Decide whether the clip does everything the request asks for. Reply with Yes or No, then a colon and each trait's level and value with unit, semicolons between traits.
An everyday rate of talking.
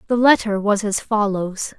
Yes: average, 170 wpm